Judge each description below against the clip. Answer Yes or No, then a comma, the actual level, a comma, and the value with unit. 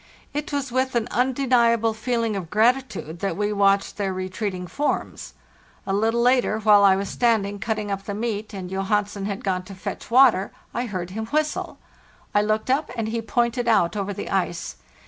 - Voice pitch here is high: Yes, high, 215 Hz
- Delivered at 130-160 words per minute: No, average, 185 wpm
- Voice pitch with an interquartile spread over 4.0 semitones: No, average, 3.2 semitones